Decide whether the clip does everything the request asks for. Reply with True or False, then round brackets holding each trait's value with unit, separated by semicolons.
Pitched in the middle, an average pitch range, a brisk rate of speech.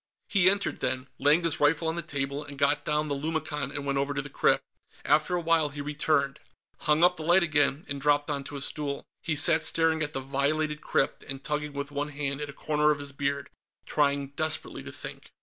False (145 Hz; 1.8 semitones; 220 wpm)